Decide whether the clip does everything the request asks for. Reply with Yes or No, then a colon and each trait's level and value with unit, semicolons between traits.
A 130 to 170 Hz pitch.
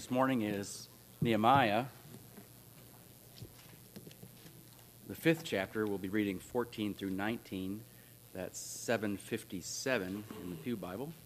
No: low, 105 Hz